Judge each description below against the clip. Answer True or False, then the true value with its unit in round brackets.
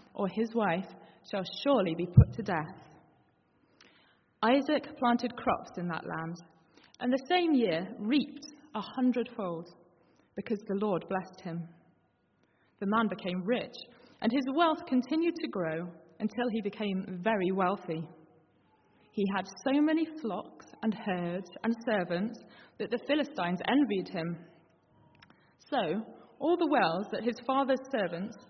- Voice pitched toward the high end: True (215 Hz)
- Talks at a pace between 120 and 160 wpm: True (135 wpm)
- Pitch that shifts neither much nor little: False (6.4 semitones)